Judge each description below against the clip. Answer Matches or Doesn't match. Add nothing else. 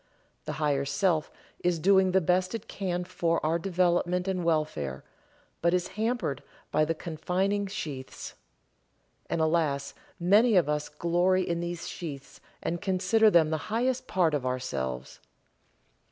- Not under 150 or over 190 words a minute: Doesn't match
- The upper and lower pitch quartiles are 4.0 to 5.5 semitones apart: Doesn't match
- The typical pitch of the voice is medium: Matches